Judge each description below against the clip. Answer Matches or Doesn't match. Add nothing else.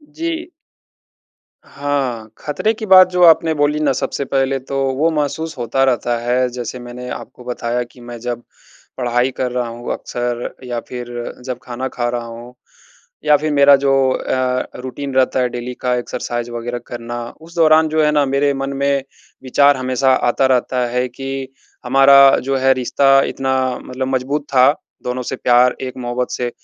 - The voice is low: Matches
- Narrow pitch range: Matches